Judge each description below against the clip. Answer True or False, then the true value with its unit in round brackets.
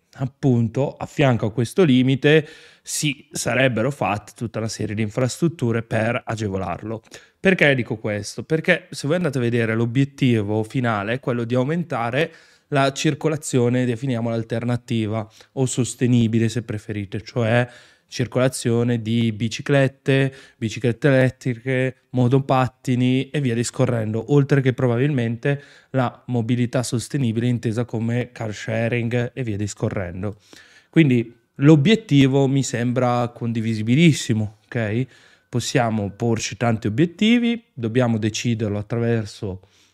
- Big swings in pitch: False (3.0 semitones)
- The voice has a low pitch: True (120 Hz)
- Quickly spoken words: False (115 wpm)